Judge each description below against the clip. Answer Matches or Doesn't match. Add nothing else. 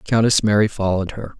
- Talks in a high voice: Doesn't match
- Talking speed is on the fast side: Doesn't match